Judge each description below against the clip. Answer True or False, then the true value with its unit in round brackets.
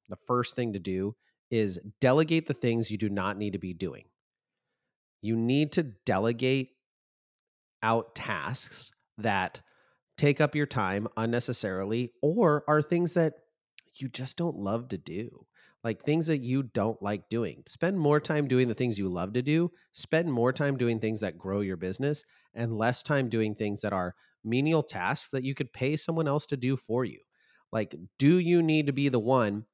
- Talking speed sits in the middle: True (185 wpm)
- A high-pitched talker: False (125 Hz)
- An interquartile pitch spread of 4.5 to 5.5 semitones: True (5.2 semitones)